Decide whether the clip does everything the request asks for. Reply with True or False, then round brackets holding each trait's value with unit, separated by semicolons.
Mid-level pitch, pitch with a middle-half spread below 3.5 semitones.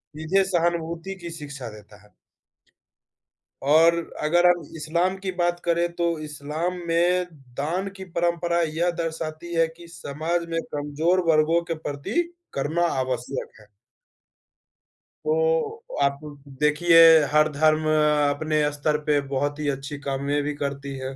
True (160 Hz; 3.1 semitones)